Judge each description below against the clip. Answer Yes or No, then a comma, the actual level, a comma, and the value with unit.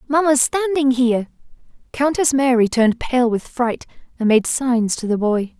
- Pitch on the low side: No, very high, 250 Hz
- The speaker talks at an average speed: Yes, average, 160 wpm